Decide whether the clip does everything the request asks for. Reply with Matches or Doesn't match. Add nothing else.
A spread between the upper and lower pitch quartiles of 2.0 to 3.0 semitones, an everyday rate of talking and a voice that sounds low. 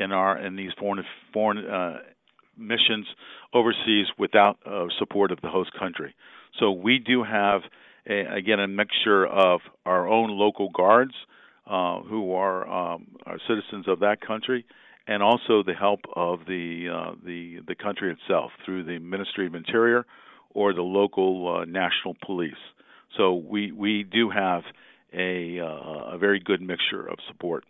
Matches